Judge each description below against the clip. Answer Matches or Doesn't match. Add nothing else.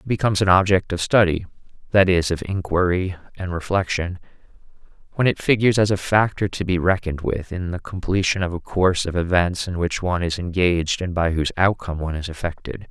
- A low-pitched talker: Matches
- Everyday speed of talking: Matches